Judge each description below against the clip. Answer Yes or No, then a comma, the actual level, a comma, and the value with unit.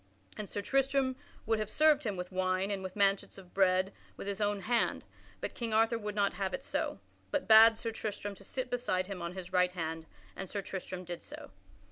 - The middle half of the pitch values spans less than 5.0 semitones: Yes, average, 3.4 semitones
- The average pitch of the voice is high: Yes, high, 200 Hz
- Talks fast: Yes, fast, 215 wpm